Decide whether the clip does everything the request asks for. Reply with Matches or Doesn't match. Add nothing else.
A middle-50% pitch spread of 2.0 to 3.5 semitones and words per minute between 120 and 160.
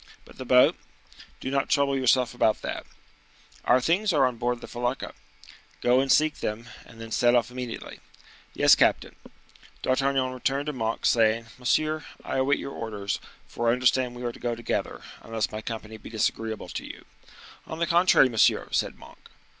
Doesn't match